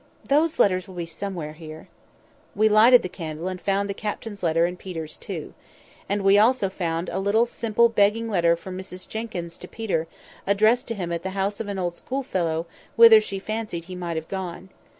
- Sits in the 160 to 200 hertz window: Yes, high, 190 Hz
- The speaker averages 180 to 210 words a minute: Yes, average, 195 wpm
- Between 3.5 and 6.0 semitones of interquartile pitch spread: Yes, average, 3.9 semitones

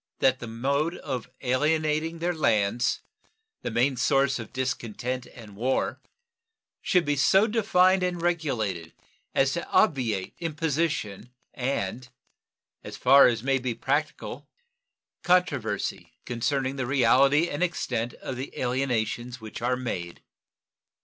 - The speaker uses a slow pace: Yes, slow, 125 wpm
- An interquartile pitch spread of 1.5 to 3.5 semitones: No, average, 4.5 semitones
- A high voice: No, low, 130 Hz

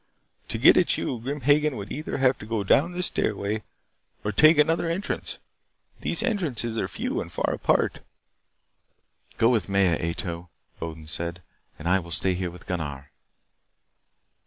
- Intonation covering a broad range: Yes, wide, 8.9 semitones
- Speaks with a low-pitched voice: Yes, low, 105 Hz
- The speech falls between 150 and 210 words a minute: Yes, average, 160 wpm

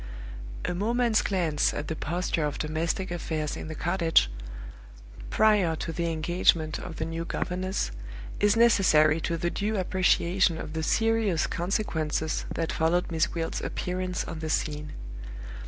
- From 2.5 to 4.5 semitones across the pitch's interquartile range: Yes, average, 2.9 semitones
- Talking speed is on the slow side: No, average, 145 wpm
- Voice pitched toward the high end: No, medium, 170 Hz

